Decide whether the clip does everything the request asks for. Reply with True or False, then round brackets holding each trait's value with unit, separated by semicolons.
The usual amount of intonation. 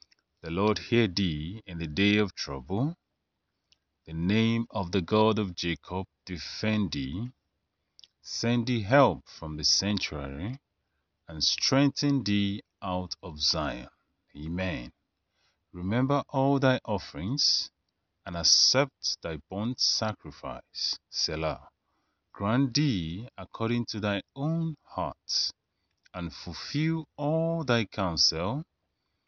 False (6.5 semitones)